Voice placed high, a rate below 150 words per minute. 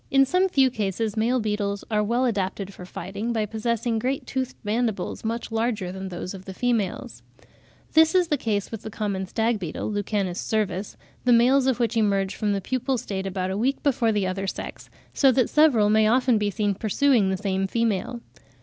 No: high, 220 Hz; average, 195 wpm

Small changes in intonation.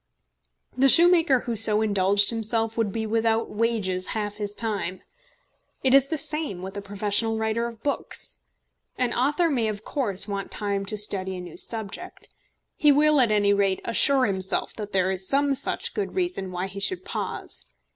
No: average, 4.4 semitones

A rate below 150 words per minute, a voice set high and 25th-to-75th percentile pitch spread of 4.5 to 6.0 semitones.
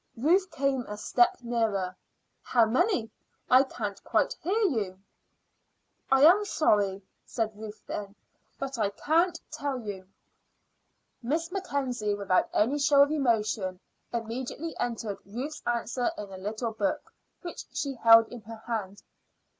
Yes: slow, 135 wpm; high, 235 Hz; average, 5.1 semitones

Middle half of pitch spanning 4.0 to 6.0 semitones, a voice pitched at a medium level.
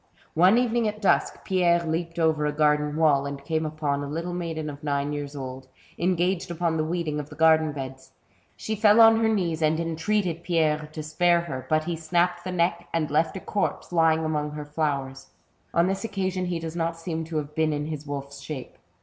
No: average, 2.8 semitones; medium, 160 Hz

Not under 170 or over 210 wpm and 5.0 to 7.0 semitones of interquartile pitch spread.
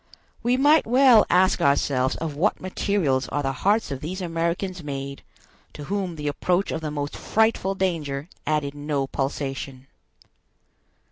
No: average, 145 wpm; average, 5.3 semitones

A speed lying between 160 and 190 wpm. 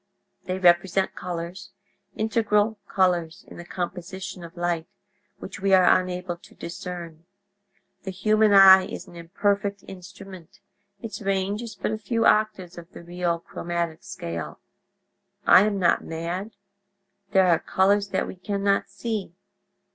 No: slow, 135 wpm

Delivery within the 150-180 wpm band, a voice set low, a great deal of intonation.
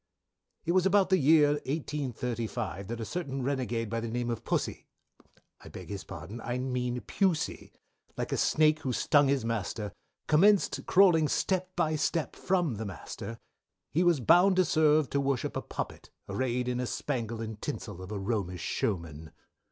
Yes: average, 170 wpm; low, 130 Hz; wide, 5.7 semitones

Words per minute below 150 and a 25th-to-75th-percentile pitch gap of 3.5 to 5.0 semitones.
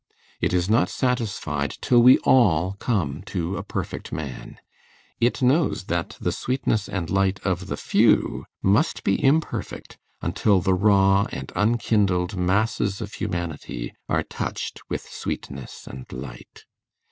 Yes: average, 140 wpm; average, 4.4 semitones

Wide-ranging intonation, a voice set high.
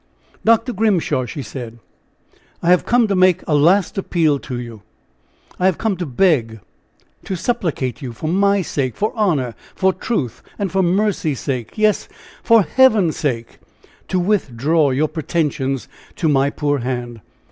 No: wide, 6.8 semitones; medium, 160 Hz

